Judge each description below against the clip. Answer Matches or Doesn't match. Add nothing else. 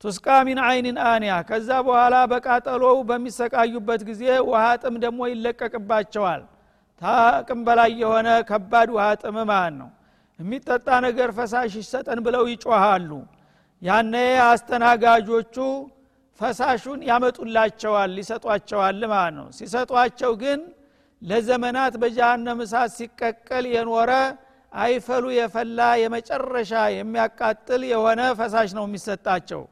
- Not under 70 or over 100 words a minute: Matches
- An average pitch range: Doesn't match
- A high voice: Matches